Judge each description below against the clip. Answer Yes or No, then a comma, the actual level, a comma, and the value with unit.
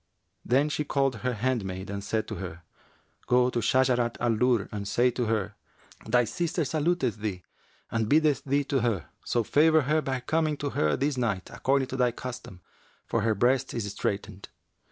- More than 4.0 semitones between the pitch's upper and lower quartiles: Yes, average, 4.4 semitones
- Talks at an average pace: Yes, average, 180 wpm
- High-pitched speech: No, low, 125 Hz